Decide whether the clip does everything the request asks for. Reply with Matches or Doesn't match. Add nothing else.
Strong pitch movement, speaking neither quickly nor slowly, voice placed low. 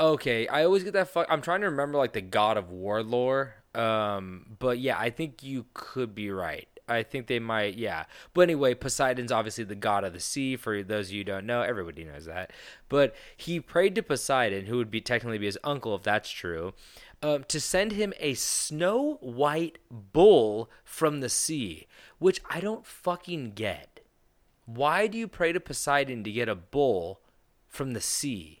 Matches